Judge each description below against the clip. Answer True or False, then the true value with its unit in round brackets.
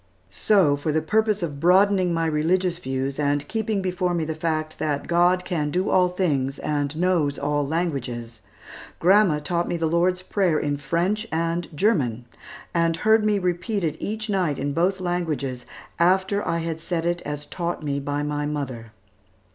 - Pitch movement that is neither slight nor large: True (3.8 semitones)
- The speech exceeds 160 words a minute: True (170 wpm)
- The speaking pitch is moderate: True (165 Hz)